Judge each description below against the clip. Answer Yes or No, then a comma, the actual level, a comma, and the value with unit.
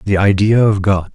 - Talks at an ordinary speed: No, fast, 210 wpm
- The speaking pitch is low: Yes, low, 100 Hz